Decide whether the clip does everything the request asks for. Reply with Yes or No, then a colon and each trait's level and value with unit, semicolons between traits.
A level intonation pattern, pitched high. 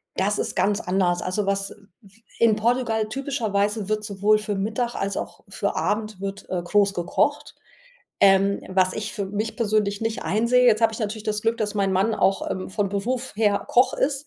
Yes: narrow, 2.2 semitones; high, 210 Hz